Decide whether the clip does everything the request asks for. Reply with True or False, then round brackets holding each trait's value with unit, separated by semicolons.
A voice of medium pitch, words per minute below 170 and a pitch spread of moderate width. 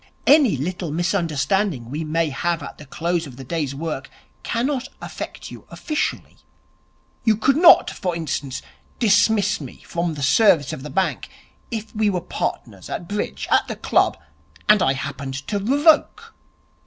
False (175 Hz; 155 wpm; 6.6 semitones)